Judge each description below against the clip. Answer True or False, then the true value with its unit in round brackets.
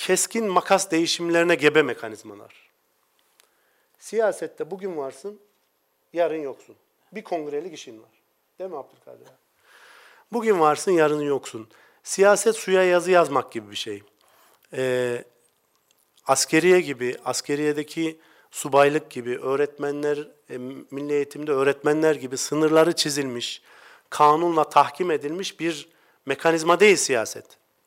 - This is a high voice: False (155 Hz)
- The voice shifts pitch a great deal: False (4.6 semitones)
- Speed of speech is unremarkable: True (105 wpm)